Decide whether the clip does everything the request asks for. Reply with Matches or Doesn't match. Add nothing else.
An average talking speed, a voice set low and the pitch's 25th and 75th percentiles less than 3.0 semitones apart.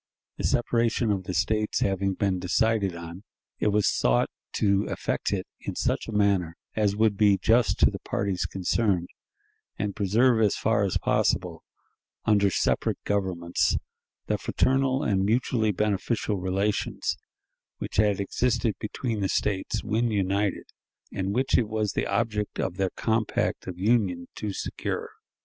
Matches